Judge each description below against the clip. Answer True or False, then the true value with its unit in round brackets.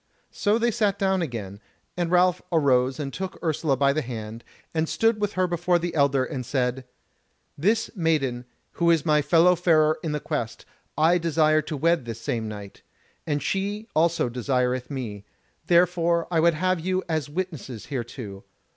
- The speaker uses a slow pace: False (170 wpm)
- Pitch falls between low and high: True (155 Hz)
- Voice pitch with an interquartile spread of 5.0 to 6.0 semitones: True (5.3 semitones)